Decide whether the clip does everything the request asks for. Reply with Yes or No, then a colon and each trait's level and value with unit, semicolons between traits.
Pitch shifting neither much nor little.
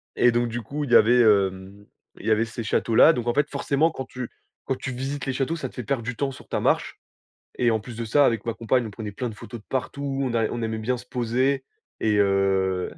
Yes: average, 3.3 semitones